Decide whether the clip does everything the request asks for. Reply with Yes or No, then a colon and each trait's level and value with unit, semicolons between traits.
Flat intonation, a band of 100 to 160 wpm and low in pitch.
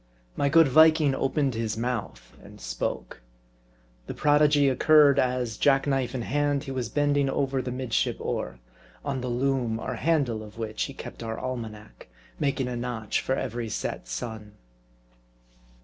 No: average, 3.8 semitones; average, 150 wpm; low, 130 Hz